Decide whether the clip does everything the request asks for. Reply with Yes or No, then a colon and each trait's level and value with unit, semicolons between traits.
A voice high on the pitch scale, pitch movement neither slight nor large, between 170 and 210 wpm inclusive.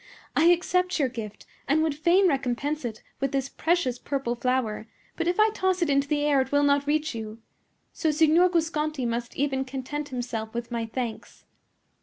Yes: very high, 280 Hz; average, 4.4 semitones; average, 185 wpm